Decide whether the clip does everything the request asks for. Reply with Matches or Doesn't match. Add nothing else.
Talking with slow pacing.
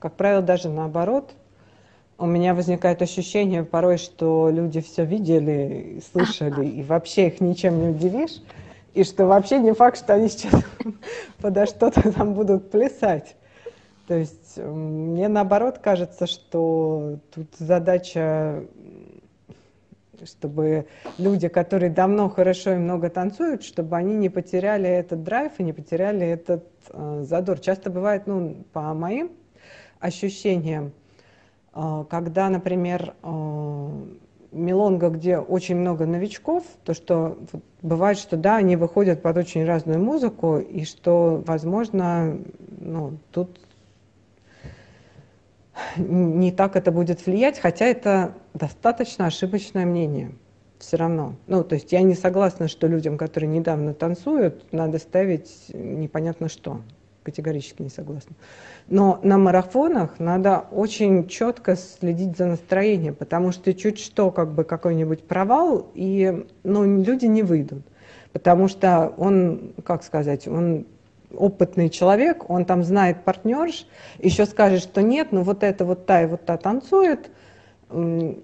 Doesn't match